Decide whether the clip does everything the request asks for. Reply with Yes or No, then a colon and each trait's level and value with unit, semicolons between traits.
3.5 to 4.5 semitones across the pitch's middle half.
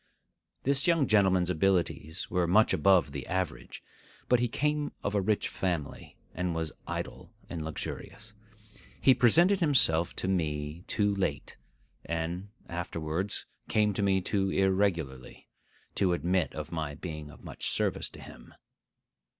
Yes: average, 4.2 semitones